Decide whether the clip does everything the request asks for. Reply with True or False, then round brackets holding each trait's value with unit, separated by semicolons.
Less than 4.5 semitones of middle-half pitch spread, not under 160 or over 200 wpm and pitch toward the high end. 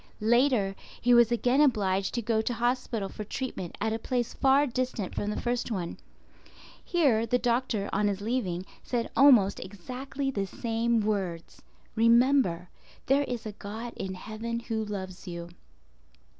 False (3.7 semitones; 150 wpm; 225 Hz)